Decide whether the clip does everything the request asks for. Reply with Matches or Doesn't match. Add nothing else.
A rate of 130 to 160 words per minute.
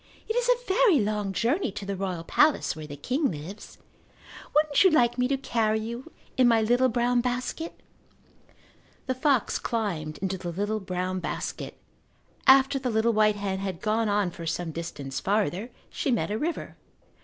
Doesn't match